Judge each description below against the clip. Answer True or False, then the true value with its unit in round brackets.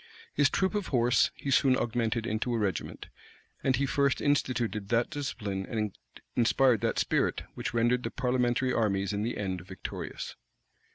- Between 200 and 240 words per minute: False (160 wpm)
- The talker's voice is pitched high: False (120 Hz)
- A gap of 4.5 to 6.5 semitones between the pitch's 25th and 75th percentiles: False (3.3 semitones)